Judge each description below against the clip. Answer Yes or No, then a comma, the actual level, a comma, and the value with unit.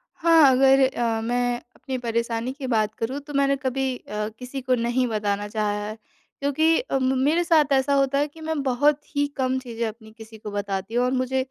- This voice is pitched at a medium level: No, very high, 255 Hz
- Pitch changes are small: No, average, 3.5 semitones